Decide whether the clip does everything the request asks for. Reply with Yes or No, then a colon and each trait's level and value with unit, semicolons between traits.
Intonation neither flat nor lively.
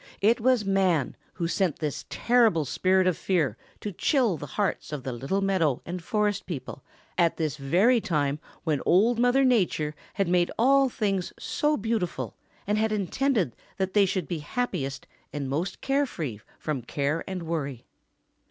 No: wide, 6.1 semitones